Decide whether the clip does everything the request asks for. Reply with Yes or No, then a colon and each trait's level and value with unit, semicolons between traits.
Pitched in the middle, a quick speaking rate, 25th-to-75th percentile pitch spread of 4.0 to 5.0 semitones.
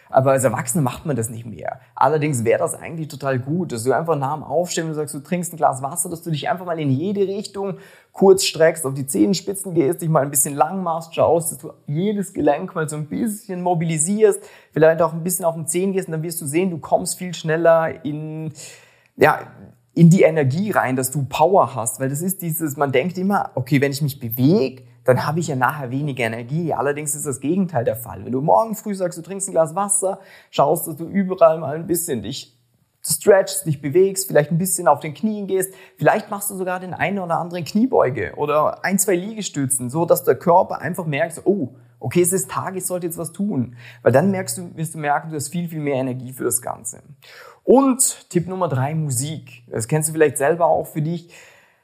Yes: medium, 160 Hz; fast, 225 wpm; average, 4.6 semitones